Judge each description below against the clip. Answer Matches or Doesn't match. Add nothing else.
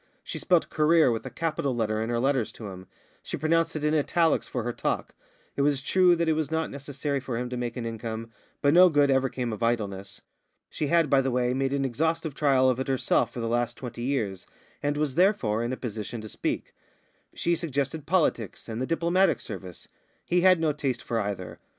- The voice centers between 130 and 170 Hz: Matches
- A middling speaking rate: Doesn't match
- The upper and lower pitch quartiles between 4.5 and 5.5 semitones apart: Matches